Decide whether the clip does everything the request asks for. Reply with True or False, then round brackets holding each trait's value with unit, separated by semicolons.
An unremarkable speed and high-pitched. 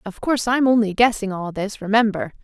True (195 wpm; 215 Hz)